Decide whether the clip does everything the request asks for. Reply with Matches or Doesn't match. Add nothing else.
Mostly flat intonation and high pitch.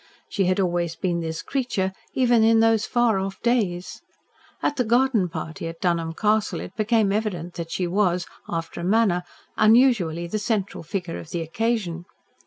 Doesn't match